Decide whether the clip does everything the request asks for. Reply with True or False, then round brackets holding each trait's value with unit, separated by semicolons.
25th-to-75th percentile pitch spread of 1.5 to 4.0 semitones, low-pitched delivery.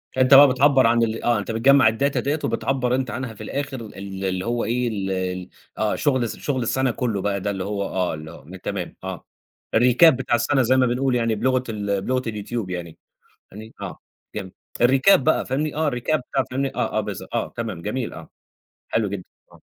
False (4.5 semitones; 115 Hz)